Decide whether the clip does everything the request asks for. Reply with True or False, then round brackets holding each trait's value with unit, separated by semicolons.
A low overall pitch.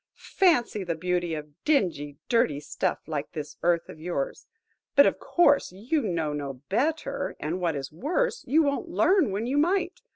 False (195 Hz)